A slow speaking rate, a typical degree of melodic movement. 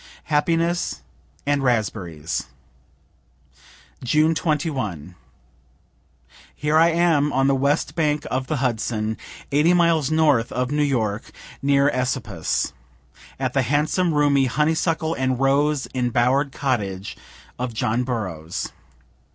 Yes: slow, 110 wpm; average, 4.2 semitones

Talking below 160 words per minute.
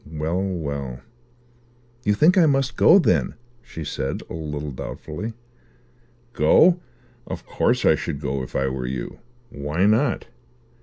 Yes: average, 140 wpm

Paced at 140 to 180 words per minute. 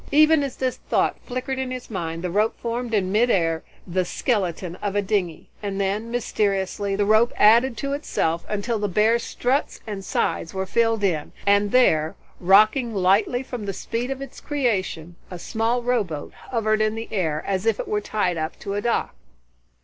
No: average, 190 wpm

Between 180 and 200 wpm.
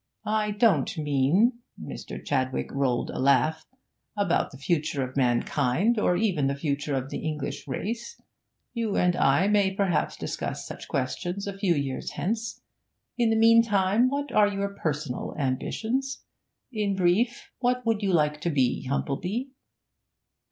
No: average, 145 wpm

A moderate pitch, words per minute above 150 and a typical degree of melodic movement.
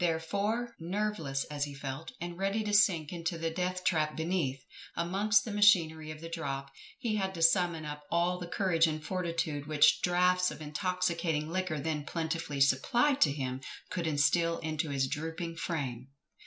Yes: medium, 165 Hz; average, 170 wpm; average, 3.4 semitones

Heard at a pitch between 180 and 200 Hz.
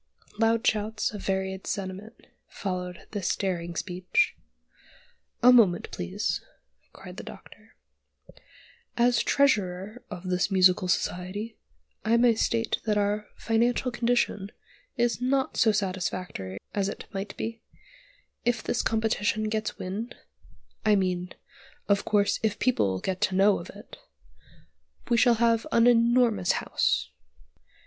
No: high, 210 Hz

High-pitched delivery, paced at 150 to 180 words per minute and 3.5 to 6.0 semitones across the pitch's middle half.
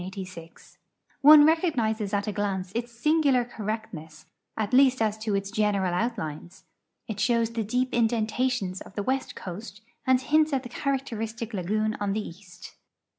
Yes: high, 220 Hz; average, 160 wpm; average, 3.9 semitones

